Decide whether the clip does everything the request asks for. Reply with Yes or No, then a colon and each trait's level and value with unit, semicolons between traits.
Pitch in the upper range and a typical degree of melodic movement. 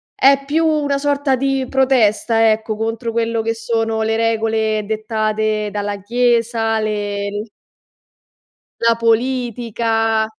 No: high, 225 Hz; narrow, 1.9 semitones